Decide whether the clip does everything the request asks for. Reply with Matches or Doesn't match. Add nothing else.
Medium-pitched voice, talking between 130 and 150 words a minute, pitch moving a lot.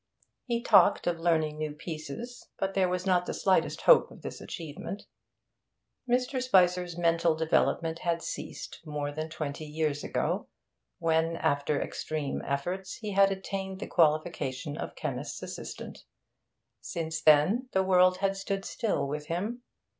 Doesn't match